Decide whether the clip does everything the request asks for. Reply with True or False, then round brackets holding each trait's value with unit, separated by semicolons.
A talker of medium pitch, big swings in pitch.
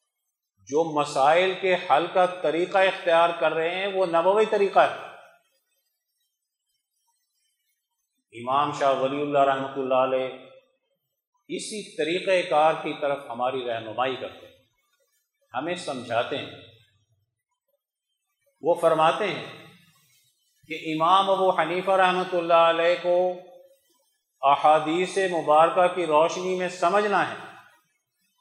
True (175 Hz; 6.0 semitones)